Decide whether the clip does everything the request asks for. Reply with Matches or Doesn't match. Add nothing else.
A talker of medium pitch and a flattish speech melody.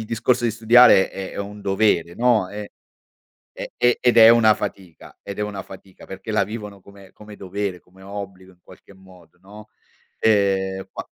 Doesn't match